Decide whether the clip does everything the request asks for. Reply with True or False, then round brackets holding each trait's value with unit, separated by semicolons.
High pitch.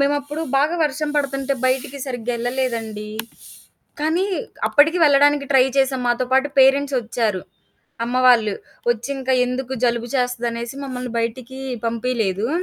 True (255 Hz)